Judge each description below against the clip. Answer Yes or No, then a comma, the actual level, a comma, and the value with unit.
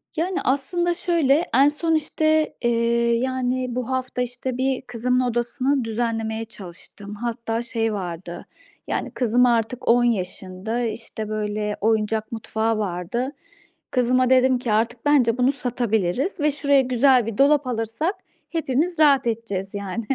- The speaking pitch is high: Yes, high, 240 Hz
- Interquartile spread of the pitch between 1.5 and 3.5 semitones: Yes, average, 3.1 semitones